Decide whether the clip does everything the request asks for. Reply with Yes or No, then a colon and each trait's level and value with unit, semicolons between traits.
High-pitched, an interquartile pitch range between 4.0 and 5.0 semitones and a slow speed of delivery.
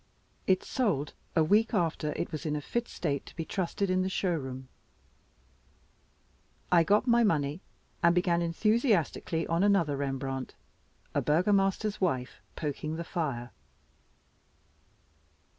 No: medium, 170 Hz; average, 4.7 semitones; slow, 125 wpm